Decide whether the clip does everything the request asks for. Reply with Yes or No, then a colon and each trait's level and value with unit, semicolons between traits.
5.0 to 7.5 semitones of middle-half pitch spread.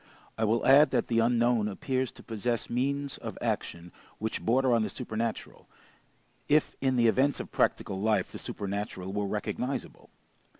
No: average, 3.6 semitones